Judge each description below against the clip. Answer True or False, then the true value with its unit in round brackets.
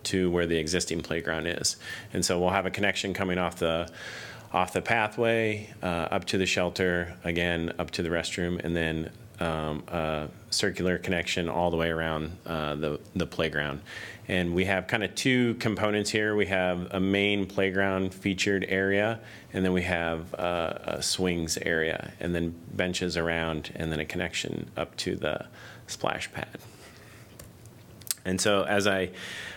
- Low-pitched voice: True (90 Hz)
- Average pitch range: True (3.3 semitones)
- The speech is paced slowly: False (165 wpm)